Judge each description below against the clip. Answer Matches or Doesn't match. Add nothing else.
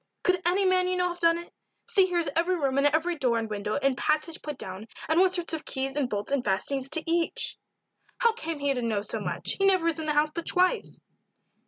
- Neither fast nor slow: Doesn't match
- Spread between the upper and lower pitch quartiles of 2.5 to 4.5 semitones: Doesn't match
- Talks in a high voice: Matches